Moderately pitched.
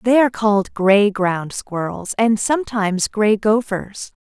No: high, 210 Hz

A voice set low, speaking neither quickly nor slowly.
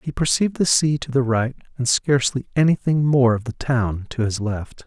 No: low, 130 Hz; fast, 210 wpm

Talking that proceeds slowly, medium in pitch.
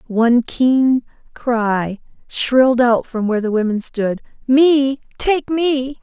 No: slow, 130 wpm; very high, 250 Hz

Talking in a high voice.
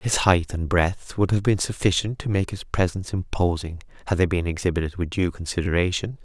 No: very low, 90 Hz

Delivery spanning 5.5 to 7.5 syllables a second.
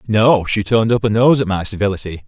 Yes: 6.1 syllables/s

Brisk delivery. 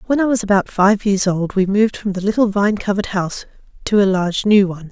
Yes: fast, 245 wpm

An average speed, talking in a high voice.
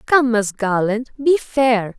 Yes: average, 150 wpm; high, 235 Hz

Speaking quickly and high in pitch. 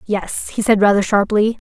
No: average, 180 wpm; high, 210 Hz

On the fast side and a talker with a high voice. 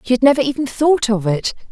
Yes: fast, 245 wpm; very high, 250 Hz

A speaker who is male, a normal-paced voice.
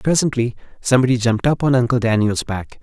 Yes: male; average, 170 wpm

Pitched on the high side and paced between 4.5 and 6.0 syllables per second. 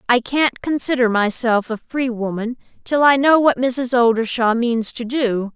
No: high, 245 Hz; 4.3 syllables/s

